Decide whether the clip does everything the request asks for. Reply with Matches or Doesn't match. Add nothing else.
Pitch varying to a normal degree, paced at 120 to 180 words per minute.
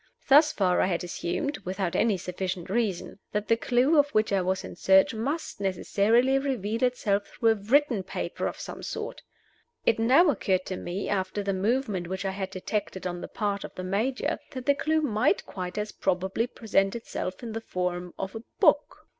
Doesn't match